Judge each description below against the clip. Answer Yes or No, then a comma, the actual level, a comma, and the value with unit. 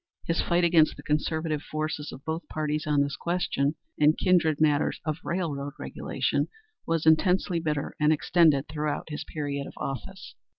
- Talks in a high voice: No, medium, 155 Hz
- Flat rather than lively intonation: Yes, narrow, 2.1 semitones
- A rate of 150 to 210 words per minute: Yes, average, 160 wpm